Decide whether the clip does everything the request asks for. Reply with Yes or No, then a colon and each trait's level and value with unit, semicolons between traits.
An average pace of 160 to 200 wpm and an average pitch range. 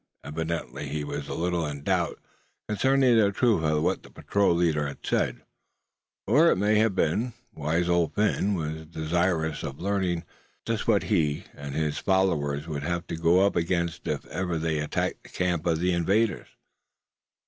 Yes: average, 170 wpm; average, 3.9 semitones